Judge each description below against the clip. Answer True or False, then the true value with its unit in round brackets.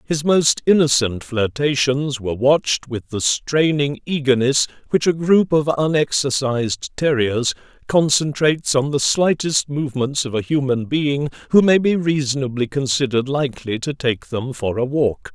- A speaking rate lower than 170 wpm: True (145 wpm)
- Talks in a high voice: False (140 Hz)